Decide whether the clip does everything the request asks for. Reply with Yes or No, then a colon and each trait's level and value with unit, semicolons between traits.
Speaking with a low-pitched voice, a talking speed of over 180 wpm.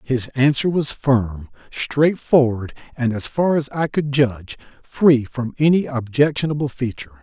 No: low, 130 Hz; average, 140 wpm